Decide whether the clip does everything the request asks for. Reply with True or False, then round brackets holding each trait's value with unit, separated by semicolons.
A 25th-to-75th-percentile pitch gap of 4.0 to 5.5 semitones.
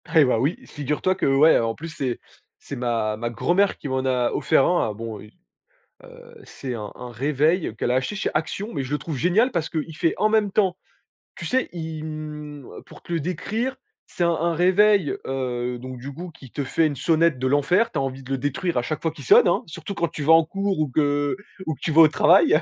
True (4.7 semitones)